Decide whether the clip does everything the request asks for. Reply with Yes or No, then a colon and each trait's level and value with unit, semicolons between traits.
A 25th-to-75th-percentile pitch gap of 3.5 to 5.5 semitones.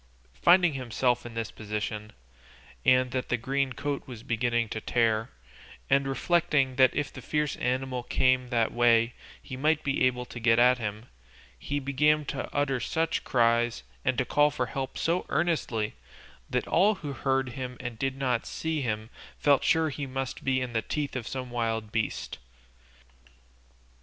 No: average, 3.0 semitones